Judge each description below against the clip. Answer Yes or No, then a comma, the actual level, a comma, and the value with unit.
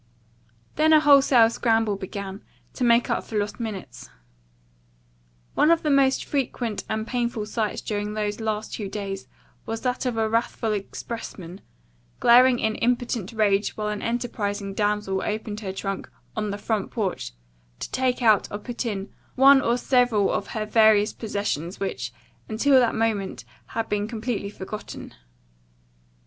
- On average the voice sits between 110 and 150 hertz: No, high, 220 Hz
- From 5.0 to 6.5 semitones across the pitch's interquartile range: No, average, 2.7 semitones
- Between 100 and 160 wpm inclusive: Yes, average, 150 wpm